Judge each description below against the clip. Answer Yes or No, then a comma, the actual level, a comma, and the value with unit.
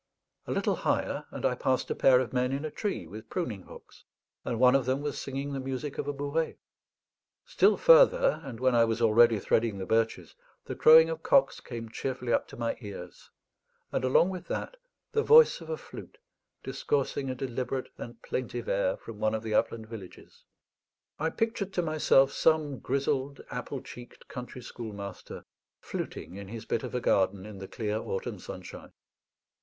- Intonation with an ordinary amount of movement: Yes, average, 4.3 semitones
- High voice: No, low, 125 Hz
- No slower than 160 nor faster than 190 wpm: Yes, average, 180 wpm